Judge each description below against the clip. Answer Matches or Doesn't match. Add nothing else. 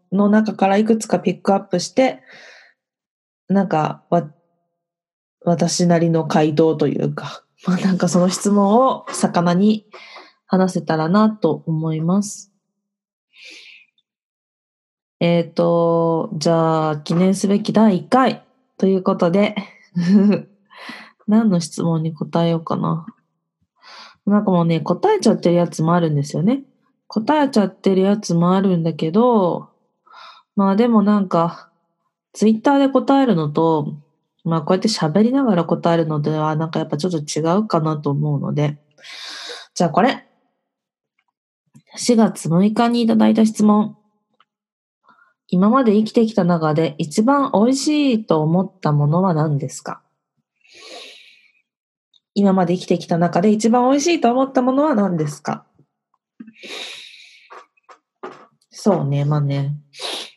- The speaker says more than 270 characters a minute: Doesn't match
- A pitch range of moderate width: Matches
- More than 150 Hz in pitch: Matches